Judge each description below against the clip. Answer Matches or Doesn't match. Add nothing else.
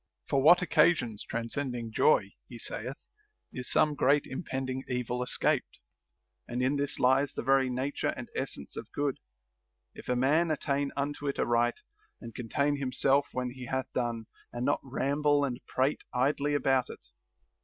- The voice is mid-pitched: Doesn't match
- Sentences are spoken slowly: Doesn't match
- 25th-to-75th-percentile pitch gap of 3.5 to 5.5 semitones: Doesn't match